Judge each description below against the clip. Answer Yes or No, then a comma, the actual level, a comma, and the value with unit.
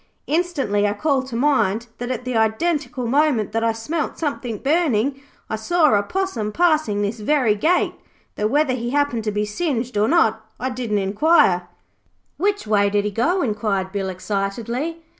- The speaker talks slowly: No, average, 170 wpm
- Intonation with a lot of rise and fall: Yes, wide, 6.1 semitones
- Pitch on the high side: Yes, high, 235 Hz